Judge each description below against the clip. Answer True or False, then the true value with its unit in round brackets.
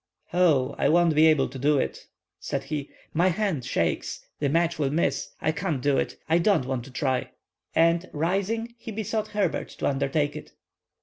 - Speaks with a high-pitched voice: False (155 Hz)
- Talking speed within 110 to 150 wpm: False (170 wpm)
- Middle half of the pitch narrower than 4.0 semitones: False (4.6 semitones)